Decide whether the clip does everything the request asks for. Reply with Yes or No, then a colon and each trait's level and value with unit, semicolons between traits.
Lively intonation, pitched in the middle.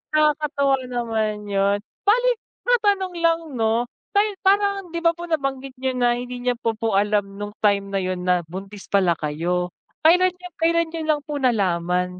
No: wide, 8.8 semitones; high, 245 Hz